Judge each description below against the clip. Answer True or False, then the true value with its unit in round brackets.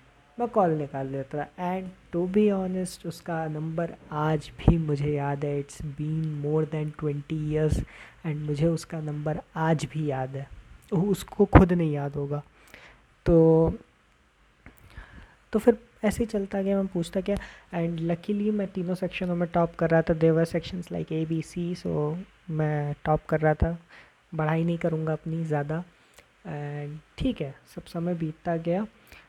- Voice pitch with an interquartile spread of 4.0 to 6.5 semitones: False (2.9 semitones)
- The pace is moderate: True (160 wpm)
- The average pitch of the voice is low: False (160 Hz)